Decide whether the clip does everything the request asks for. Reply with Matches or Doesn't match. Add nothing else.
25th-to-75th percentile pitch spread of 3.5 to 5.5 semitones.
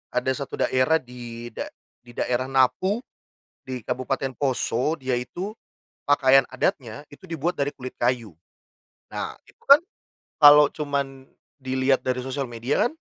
Doesn't match